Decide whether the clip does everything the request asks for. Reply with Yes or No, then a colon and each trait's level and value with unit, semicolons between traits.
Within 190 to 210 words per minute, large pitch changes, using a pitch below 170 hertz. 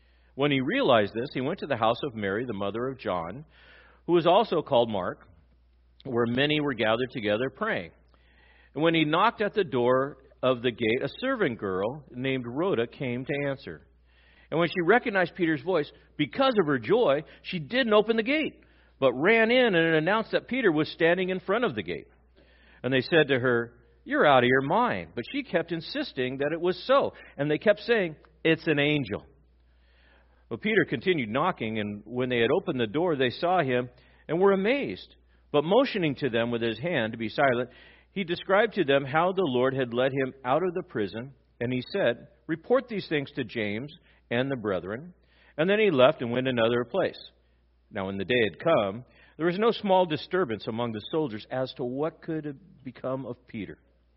Yes: average, 200 wpm; wide, 7.0 semitones; low, 135 Hz